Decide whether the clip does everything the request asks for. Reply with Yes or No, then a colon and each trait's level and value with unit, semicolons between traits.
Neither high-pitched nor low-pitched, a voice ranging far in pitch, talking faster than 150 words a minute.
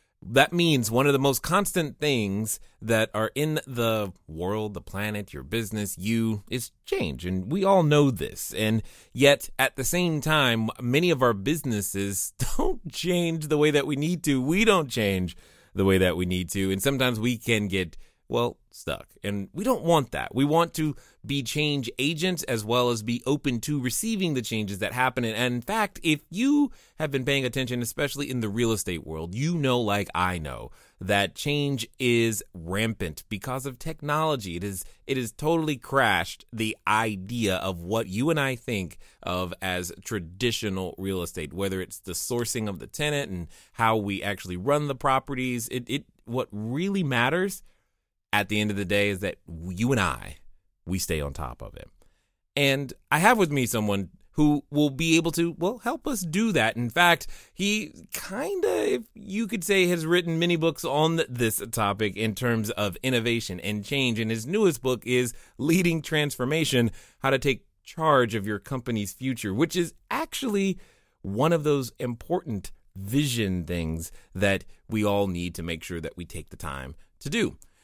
No: low, 120 Hz; wide, 6.8 semitones; average, 185 wpm